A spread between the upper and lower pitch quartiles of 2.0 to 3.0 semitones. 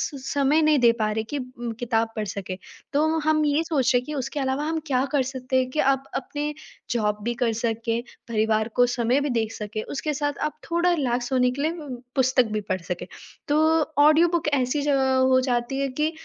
No: average, 3.8 semitones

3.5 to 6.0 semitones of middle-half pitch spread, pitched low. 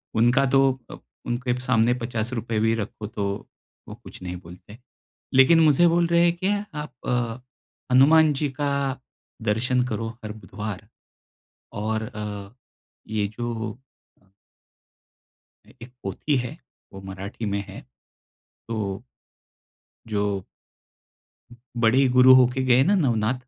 Yes: average, 4.0 semitones; low, 120 Hz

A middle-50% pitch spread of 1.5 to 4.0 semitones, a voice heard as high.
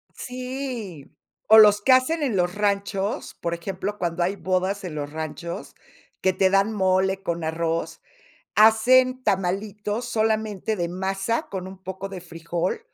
Yes: average, 3.5 semitones; high, 195 Hz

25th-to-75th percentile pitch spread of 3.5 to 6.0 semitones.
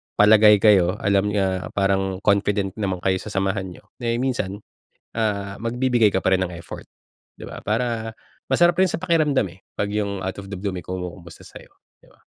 No: average, 2.8 semitones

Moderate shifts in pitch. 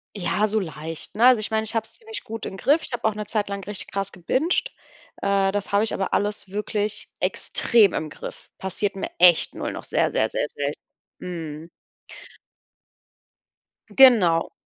Yes: average, 3.4 semitones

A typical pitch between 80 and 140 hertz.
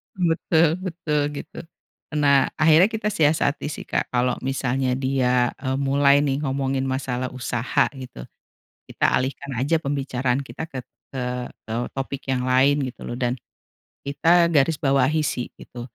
Yes: low, 135 Hz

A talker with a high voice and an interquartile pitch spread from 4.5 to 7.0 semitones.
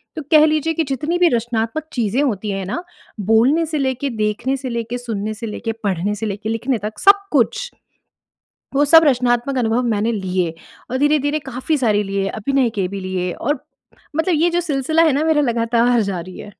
Yes: high, 240 Hz; wide, 5.6 semitones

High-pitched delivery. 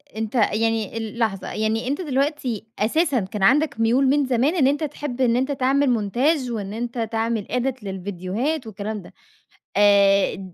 Yes: high, 230 Hz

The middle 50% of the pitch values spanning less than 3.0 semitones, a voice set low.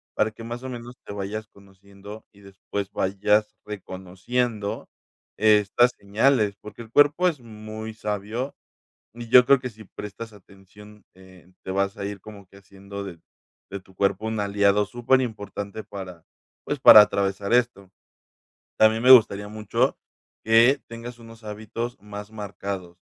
Yes: narrow, 2.5 semitones; low, 105 Hz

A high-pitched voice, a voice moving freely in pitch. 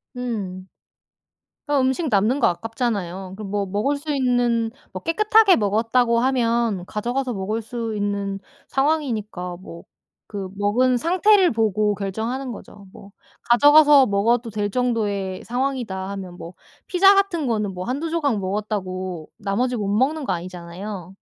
No: high, 225 Hz; average, 4.8 semitones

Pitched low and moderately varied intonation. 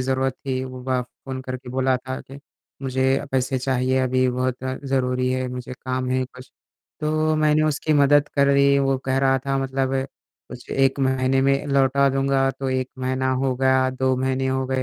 No: low, 130 Hz; narrow, 1.0 semitones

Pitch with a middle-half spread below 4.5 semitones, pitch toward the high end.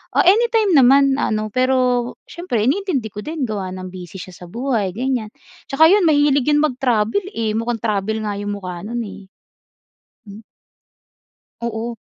No: average, 5.2 semitones; high, 235 Hz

